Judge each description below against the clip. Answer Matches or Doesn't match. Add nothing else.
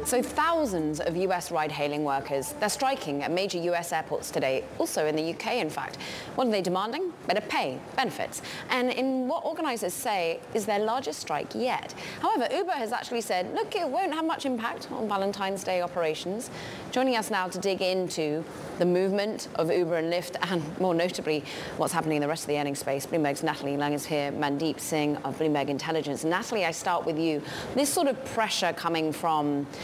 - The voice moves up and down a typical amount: Doesn't match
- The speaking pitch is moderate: Matches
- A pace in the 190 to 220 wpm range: Matches